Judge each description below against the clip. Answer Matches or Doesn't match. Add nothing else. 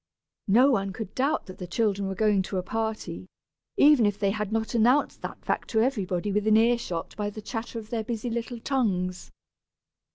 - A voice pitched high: Matches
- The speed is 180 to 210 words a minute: Matches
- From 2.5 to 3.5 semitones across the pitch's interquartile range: Matches